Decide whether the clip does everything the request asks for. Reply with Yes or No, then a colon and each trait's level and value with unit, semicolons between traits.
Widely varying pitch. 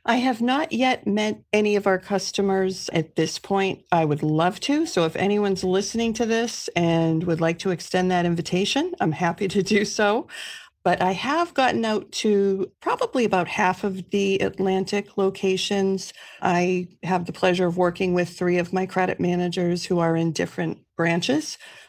No: average, 3.1 semitones